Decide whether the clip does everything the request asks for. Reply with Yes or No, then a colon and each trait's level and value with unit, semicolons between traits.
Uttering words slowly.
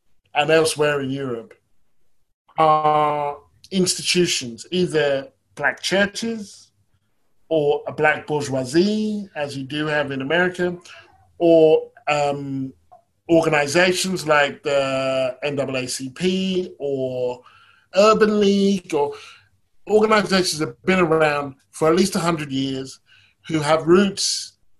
Yes: slow, 105 wpm